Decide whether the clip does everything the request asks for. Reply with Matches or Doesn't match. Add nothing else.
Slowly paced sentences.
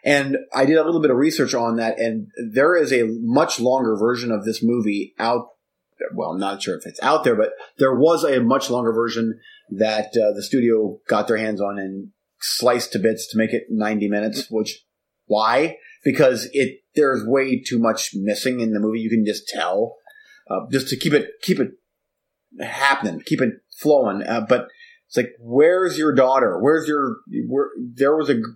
Doesn't match